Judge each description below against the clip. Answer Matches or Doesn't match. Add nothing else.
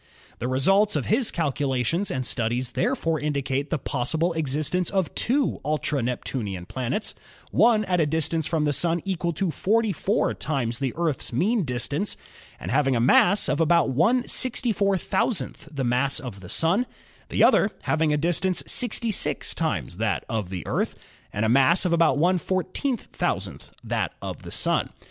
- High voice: Doesn't match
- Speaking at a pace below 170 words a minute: Matches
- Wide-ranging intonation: Matches